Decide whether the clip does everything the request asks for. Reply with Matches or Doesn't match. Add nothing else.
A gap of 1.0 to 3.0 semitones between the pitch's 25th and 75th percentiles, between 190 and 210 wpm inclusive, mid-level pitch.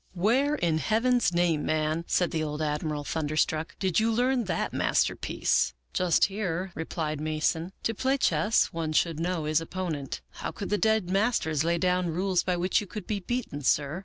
Doesn't match